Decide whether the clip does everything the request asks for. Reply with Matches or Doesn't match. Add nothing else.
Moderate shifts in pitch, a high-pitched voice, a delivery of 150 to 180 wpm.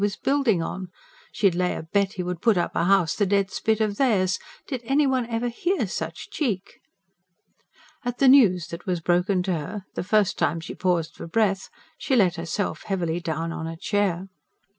Doesn't match